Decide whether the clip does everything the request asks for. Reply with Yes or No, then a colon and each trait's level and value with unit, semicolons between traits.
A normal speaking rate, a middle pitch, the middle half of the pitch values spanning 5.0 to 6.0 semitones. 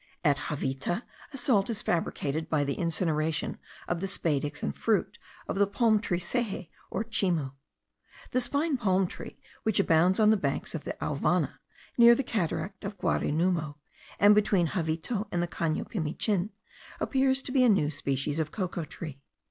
Yes: average, 165 wpm; medium, 180 Hz; average, 5.3 semitones